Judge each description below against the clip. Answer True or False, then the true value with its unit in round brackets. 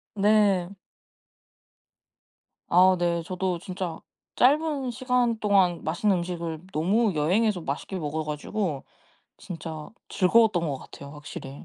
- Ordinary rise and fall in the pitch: True (4.7 semitones)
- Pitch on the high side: False (180 Hz)